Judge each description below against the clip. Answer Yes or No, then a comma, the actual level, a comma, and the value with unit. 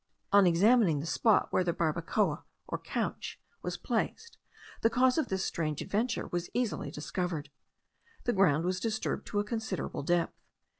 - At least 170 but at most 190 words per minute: No, average, 155 wpm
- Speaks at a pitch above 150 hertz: Yes, medium, 185 Hz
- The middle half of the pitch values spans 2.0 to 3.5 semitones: No, average, 4.8 semitones